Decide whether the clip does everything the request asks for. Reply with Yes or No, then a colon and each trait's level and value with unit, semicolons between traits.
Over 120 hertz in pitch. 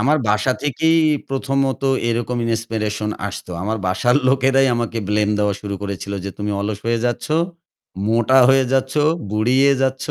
No: low, 115 Hz